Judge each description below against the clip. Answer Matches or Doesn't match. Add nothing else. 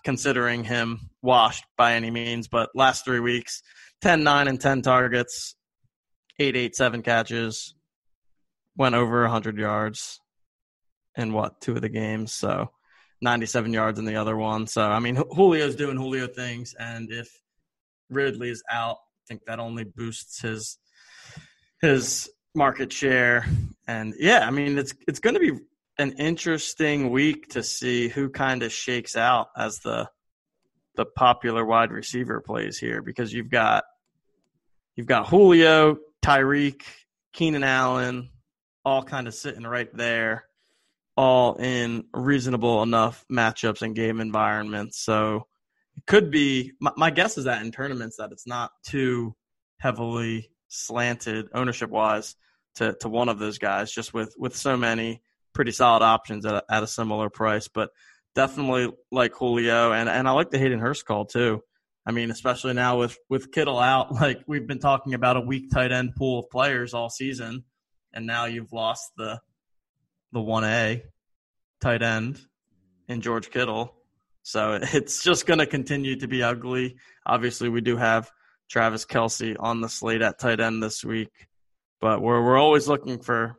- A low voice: Matches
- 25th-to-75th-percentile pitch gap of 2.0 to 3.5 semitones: Matches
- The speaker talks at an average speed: Matches